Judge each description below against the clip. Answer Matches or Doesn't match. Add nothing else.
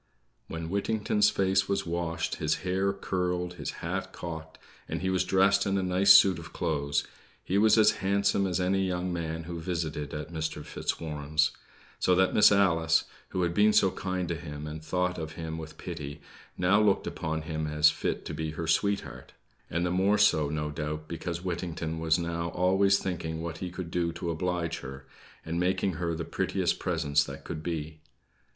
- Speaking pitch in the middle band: Doesn't match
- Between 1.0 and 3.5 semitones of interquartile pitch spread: Matches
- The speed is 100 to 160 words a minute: Doesn't match